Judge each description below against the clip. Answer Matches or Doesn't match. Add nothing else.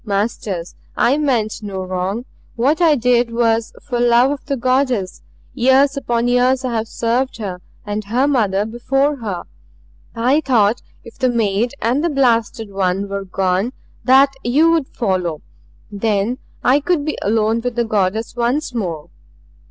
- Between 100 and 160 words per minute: Matches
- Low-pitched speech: Doesn't match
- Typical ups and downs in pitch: Matches